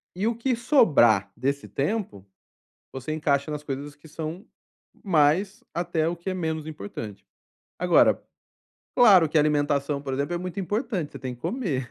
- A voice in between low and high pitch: Yes, medium, 155 Hz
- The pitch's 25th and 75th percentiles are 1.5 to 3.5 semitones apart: No, average, 4.9 semitones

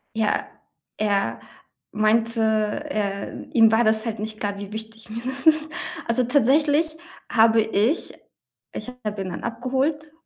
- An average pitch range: Yes, average, 3.5 semitones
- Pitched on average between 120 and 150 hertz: No, high, 225 Hz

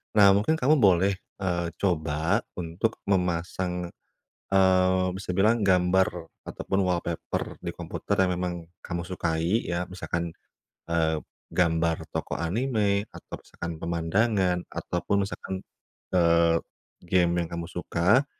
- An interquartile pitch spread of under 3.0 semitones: Yes, narrow, 2.4 semitones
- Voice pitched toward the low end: Yes, very low, 90 Hz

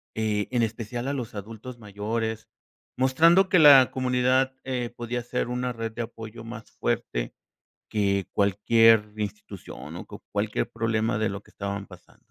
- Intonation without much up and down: No, average, 3.0 semitones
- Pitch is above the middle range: No, low, 115 Hz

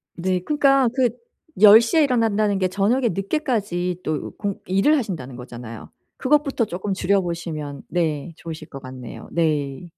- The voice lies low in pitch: No, medium, 185 Hz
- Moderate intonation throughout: No, wide, 6.7 semitones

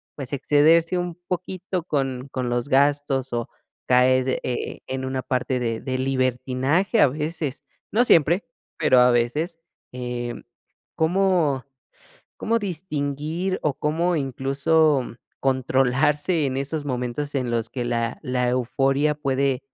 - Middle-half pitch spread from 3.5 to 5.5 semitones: Yes, average, 3.8 semitones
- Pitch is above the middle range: No, low, 135 Hz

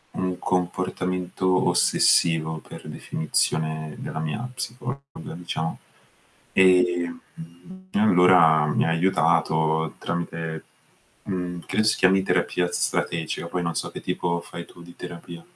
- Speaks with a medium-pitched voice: No, very low, 85 Hz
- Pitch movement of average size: No, narrow, 2.1 semitones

